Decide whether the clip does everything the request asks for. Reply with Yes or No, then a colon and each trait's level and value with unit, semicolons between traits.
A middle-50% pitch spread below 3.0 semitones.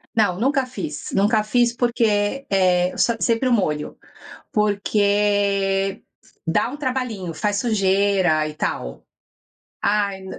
No: average, 3.4 semitones